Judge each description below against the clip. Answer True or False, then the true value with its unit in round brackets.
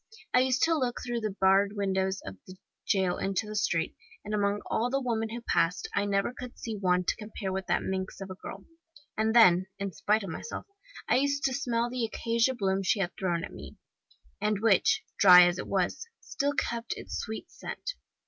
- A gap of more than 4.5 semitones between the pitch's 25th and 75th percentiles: False (3.7 semitones)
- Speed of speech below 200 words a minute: False (205 wpm)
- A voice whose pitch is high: True (205 Hz)